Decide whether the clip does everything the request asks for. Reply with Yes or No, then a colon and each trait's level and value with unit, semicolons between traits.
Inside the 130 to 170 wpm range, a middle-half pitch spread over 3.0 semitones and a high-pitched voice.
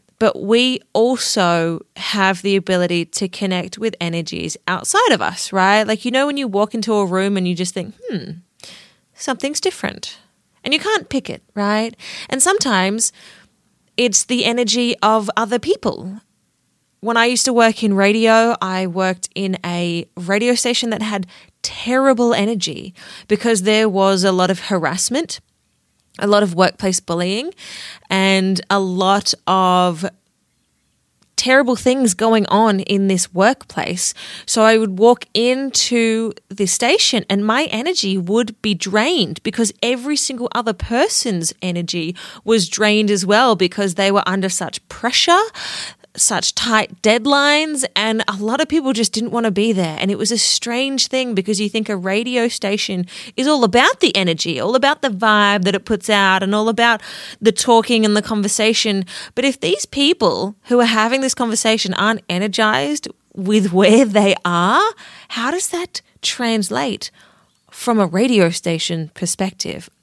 Yes: average, 160 wpm; average, 3.8 semitones; high, 215 Hz